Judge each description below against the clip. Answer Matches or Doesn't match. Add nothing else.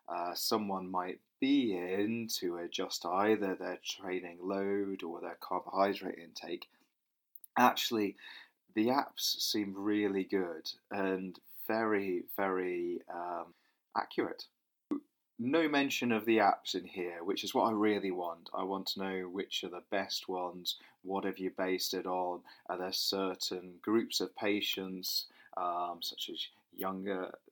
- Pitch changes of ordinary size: Doesn't match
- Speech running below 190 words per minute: Matches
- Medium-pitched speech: Doesn't match